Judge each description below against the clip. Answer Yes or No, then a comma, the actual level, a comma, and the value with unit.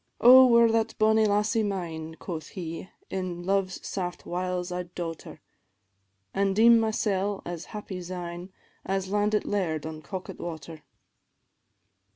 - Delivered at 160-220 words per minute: No, slow, 135 wpm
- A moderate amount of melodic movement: Yes, average, 3.2 semitones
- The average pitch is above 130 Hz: Yes, medium, 185 Hz